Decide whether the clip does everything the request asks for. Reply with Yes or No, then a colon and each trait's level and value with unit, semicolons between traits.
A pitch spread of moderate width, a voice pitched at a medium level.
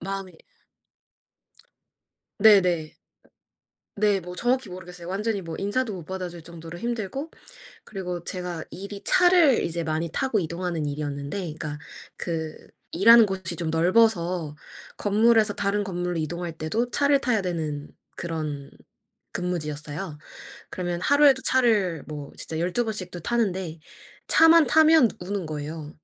Yes: average, 4.8 semitones; medium, 180 Hz